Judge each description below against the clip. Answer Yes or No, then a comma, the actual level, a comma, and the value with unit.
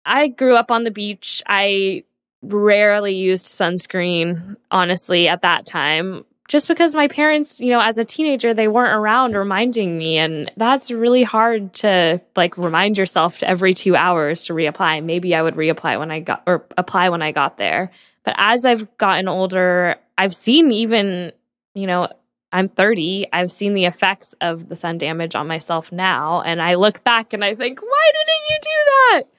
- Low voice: No, high, 190 Hz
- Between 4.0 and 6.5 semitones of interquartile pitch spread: Yes, average, 4.8 semitones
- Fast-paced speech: No, average, 185 wpm